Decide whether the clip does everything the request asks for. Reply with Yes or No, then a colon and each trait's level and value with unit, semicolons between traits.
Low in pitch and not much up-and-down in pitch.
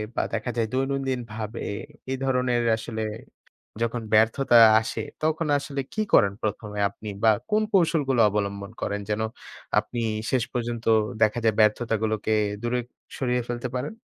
No: low, 120 Hz; average, 3.2 semitones